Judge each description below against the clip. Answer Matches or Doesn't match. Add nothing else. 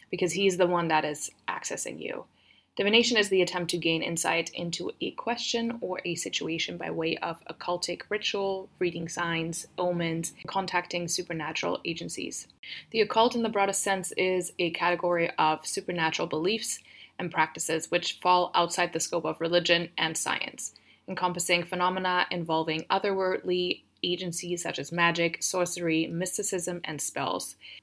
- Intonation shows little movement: Matches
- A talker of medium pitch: Matches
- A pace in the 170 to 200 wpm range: Doesn't match